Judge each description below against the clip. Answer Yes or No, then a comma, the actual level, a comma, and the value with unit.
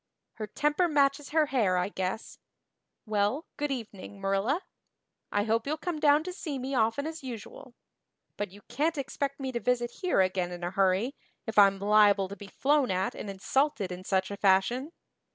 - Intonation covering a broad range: Yes, wide, 6.3 semitones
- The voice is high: Yes, high, 225 Hz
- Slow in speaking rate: No, average, 185 wpm